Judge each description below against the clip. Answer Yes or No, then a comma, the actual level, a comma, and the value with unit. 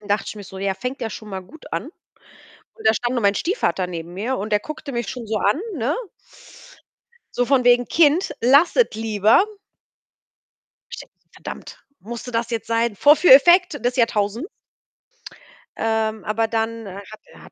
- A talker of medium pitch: No, high, 230 Hz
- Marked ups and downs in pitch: No, average, 3.8 semitones